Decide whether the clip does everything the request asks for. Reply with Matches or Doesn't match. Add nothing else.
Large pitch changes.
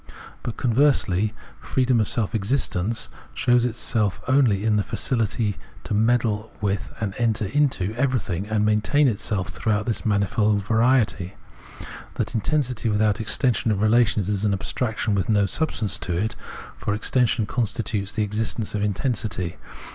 Doesn't match